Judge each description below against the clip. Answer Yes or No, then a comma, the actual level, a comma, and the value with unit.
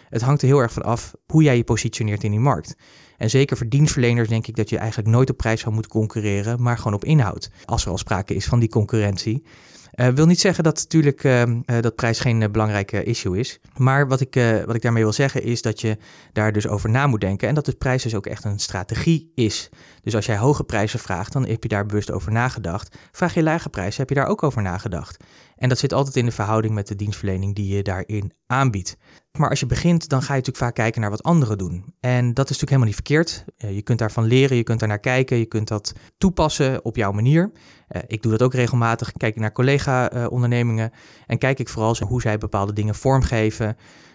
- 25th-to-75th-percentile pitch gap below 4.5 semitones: Yes, average, 3.7 semitones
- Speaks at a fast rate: Yes, fast, 240 wpm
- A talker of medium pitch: No, low, 115 Hz